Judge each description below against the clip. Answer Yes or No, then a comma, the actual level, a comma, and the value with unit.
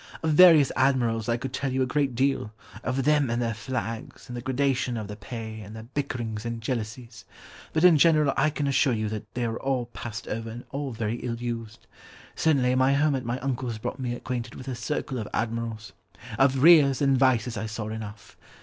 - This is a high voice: No, low, 125 Hz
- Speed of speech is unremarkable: No, fast, 210 wpm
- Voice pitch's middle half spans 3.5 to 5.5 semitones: No, average, 3.1 semitones